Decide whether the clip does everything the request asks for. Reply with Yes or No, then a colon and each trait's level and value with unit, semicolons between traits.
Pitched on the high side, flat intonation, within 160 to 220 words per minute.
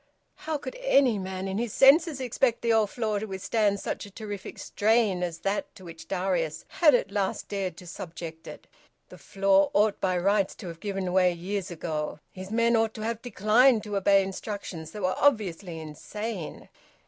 No: high, 200 Hz; average, 3.4 semitones; average, 185 wpm